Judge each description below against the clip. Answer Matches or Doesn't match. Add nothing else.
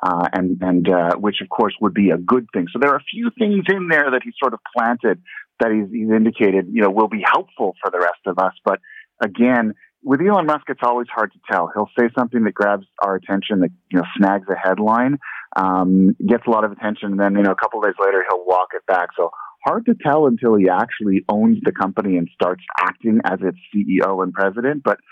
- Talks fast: Matches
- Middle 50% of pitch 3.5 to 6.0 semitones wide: Matches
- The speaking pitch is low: Matches